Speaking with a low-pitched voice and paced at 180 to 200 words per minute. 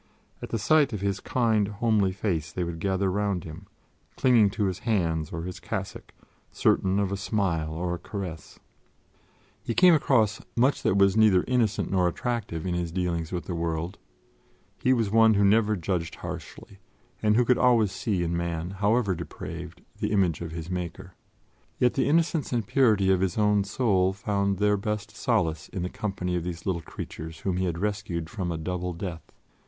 Yes: very low, 95 Hz; average, 185 wpm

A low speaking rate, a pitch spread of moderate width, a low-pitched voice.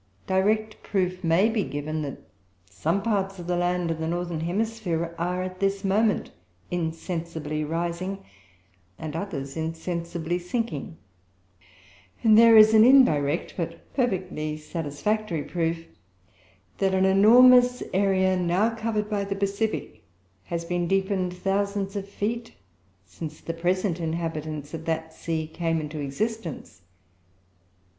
No: slow, 125 wpm; average, 3.6 semitones; medium, 180 Hz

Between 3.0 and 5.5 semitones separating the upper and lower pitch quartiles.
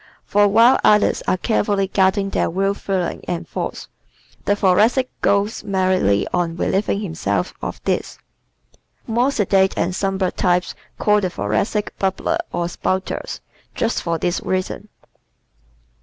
No: narrow, 2.4 semitones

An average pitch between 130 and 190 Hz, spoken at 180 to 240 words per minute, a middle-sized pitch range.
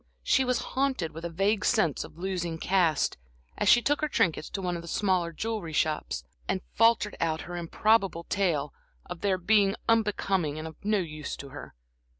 Yes: medium, 185 Hz; average, 185 wpm; average, 4.4 semitones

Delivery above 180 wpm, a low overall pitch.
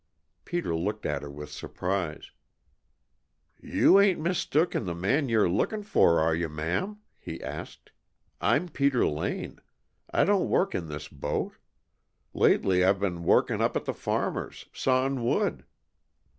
No: average, 145 wpm; low, 100 Hz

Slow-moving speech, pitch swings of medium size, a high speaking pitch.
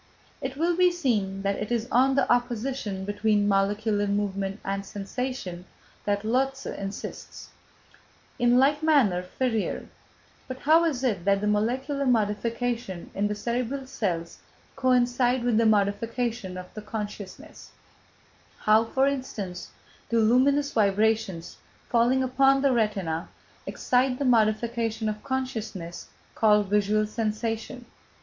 Yes: slow, 125 wpm; average, 4.0 semitones; high, 225 Hz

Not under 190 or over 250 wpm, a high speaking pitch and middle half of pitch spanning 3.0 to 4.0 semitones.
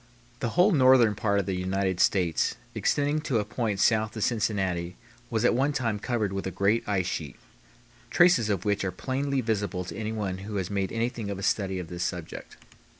No: average, 200 wpm; low, 105 Hz; average, 3.7 semitones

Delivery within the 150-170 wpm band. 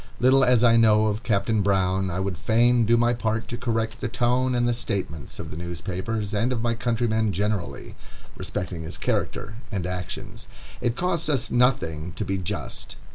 No: average, 185 wpm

